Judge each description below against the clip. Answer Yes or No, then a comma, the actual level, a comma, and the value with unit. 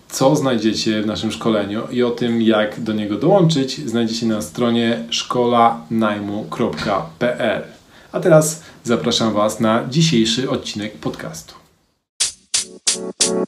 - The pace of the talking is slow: Yes, slow, 105 wpm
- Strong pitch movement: No, narrow, 2.4 semitones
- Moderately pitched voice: No, low, 115 Hz